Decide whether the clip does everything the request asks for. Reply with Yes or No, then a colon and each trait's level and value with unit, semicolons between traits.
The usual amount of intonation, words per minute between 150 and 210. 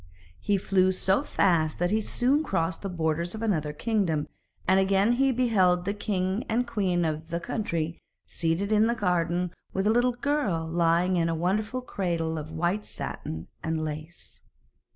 Yes: average, 4.4 semitones; average, 170 wpm